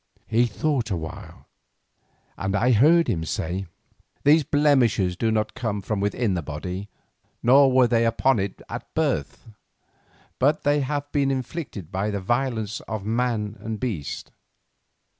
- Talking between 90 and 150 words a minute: Yes, average, 140 wpm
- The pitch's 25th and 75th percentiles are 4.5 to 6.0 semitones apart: Yes, average, 5.1 semitones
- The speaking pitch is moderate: No, low, 115 Hz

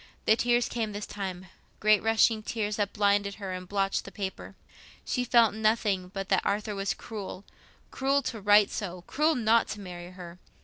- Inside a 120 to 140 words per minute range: No, average, 170 wpm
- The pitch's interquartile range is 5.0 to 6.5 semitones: No, narrow, 2.4 semitones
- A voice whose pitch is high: Yes, high, 205 Hz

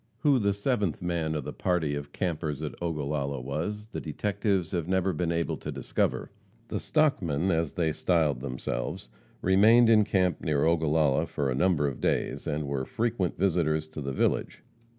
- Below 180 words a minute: Yes, average, 170 wpm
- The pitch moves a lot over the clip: No, average, 4.5 semitones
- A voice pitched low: Yes, very low, 85 Hz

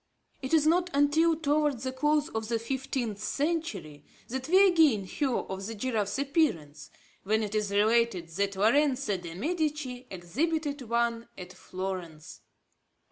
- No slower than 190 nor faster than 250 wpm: No, average, 140 wpm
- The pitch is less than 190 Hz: No, high, 240 Hz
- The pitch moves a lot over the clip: Yes, wide, 6.8 semitones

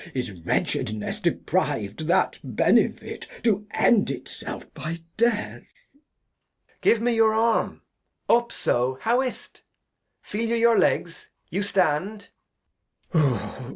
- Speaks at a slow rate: Yes, slow, 115 wpm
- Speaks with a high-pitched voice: Yes, high, 210 Hz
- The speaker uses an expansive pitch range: Yes, wide, 6.9 semitones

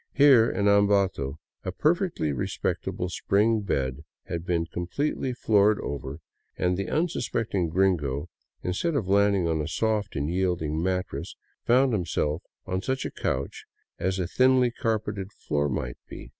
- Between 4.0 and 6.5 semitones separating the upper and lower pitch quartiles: Yes, average, 5.2 semitones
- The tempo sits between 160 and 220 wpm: No, average, 150 wpm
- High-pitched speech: No, very low, 95 Hz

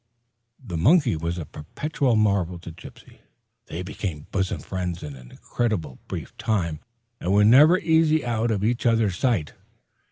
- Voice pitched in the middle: No, low, 100 Hz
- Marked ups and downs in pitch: Yes, wide, 5.9 semitones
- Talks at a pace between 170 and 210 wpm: No, average, 155 wpm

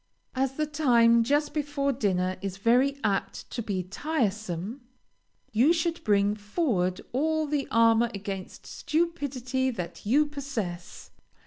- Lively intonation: Yes, wide, 6.2 semitones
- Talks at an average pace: No, slow, 125 wpm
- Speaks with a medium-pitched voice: No, high, 240 Hz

